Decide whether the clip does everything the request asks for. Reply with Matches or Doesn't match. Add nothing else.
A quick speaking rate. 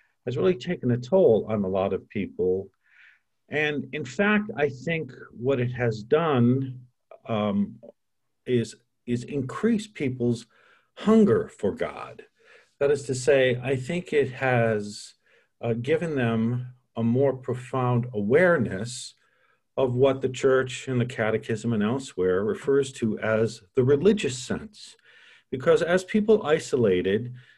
Doesn't match